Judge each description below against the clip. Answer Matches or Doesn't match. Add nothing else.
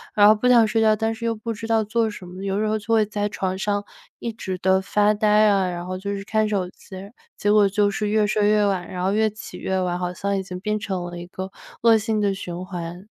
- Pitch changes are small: Matches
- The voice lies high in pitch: Matches